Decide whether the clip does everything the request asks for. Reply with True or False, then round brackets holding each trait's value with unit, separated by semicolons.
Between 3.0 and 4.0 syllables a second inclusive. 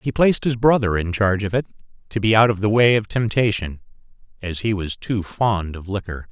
False (5.5 syllables/s)